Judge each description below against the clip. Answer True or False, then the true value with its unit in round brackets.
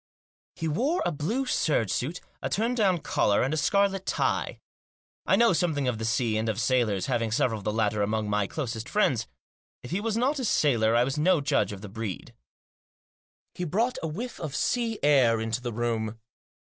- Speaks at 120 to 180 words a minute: False (195 wpm)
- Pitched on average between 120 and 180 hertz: True (135 Hz)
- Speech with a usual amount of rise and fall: False (9.0 semitones)